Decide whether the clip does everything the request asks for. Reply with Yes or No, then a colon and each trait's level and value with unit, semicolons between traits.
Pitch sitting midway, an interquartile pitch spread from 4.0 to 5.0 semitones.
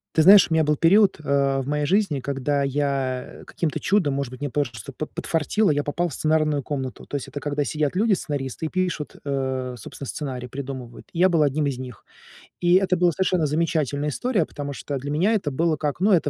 No: medium, 145 Hz; average, 3.4 semitones